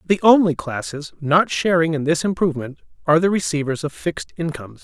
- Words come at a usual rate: Yes, average, 175 wpm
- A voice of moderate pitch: Yes, medium, 155 Hz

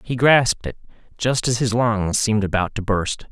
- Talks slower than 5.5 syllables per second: Yes, 5.0 syllables/s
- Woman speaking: No, male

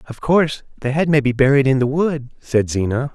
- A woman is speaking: No, male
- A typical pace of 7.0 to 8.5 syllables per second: No, 5.5 syllables/s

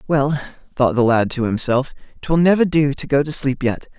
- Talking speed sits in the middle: No, fast, 210 wpm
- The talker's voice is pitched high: No, medium, 140 Hz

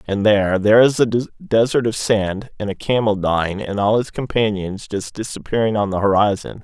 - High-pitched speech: No, low, 105 Hz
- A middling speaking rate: Yes, average, 190 wpm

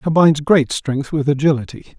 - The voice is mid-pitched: Yes, medium, 145 Hz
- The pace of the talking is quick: No, average, 150 wpm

